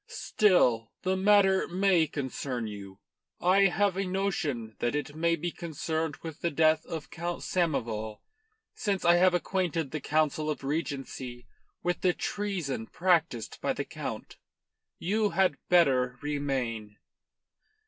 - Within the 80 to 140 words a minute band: Yes, slow, 135 wpm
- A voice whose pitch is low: No, medium, 160 Hz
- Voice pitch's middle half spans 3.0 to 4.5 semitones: No, average, 5.3 semitones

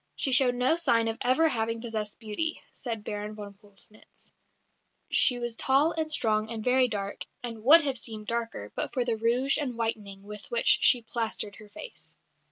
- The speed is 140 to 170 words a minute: No, average, 180 wpm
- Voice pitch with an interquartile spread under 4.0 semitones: Yes, average, 3.0 semitones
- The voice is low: No, high, 230 Hz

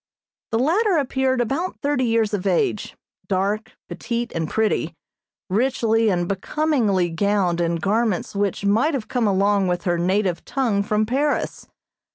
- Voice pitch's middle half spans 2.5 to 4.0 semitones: No, average, 4.8 semitones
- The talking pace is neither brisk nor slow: Yes, average, 145 wpm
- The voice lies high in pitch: Yes, high, 210 Hz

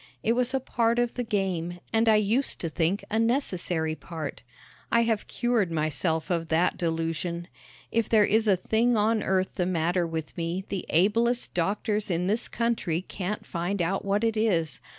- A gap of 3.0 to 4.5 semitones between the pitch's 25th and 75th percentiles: No, average, 5.0 semitones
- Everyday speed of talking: Yes, average, 180 wpm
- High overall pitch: Yes, high, 195 Hz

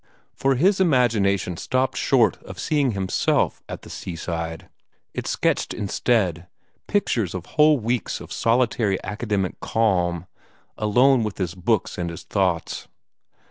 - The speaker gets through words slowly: Yes, slow, 130 wpm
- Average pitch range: No, wide, 5.7 semitones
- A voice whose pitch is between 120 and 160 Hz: No, low, 105 Hz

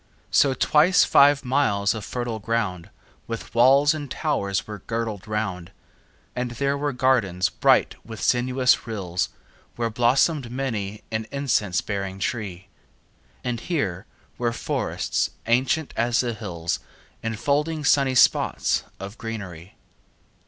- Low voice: Yes, low, 115 Hz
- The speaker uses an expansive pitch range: No, average, 4.7 semitones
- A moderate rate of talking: No, slow, 130 wpm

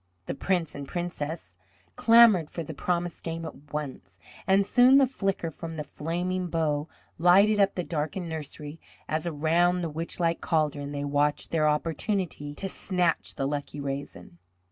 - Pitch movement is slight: No, average, 3.3 semitones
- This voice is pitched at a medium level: Yes, medium, 165 Hz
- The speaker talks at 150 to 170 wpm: Yes, average, 155 wpm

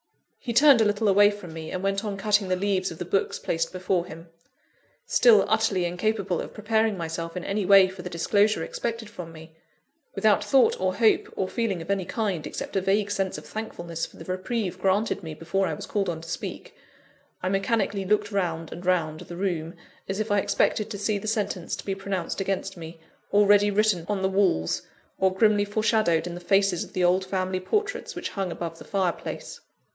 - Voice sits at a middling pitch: No, high, 195 Hz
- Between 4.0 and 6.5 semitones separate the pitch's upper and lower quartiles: No, average, 2.9 semitones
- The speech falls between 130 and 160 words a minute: No, fast, 205 wpm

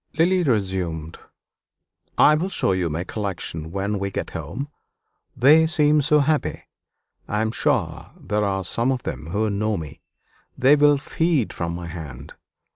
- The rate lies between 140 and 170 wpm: Yes, average, 155 wpm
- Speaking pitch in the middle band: No, low, 105 Hz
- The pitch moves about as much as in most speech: No, wide, 8.6 semitones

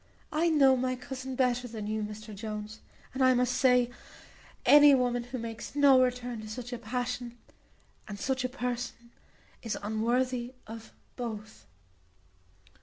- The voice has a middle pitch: No, high, 245 Hz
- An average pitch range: No, narrow, 2.3 semitones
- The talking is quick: No, average, 145 wpm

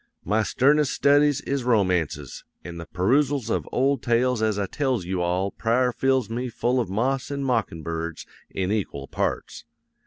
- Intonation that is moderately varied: No, wide, 6.0 semitones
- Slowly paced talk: No, average, 165 wpm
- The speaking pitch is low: Yes, low, 115 Hz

